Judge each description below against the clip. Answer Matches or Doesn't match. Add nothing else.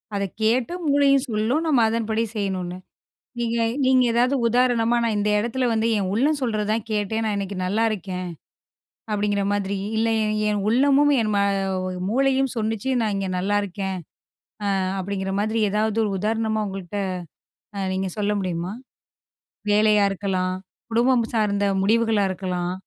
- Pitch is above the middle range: Matches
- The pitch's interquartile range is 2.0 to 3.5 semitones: Matches